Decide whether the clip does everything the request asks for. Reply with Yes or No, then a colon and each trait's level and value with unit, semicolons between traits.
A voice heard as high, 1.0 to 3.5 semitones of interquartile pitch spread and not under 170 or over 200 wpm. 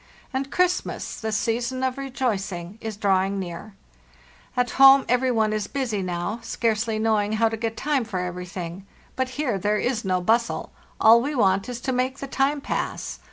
No: high, 225 Hz; average, 4.6 semitones; average, 175 wpm